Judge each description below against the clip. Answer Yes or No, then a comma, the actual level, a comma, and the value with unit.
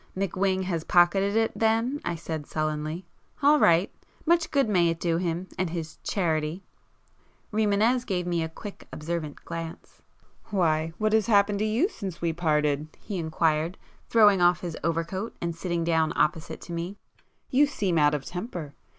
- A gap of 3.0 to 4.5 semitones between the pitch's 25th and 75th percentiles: Yes, average, 3.9 semitones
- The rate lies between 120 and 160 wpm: Yes, average, 155 wpm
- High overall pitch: No, medium, 175 Hz